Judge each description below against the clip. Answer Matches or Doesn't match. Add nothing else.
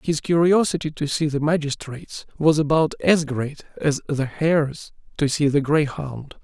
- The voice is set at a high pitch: Doesn't match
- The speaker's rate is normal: Matches